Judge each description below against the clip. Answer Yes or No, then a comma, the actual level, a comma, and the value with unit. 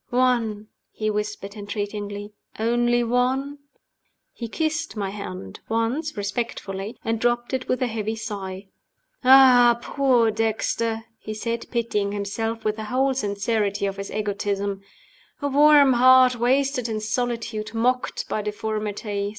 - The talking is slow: Yes, slow, 130 wpm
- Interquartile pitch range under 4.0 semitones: Yes, average, 3.2 semitones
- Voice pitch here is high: Yes, high, 225 Hz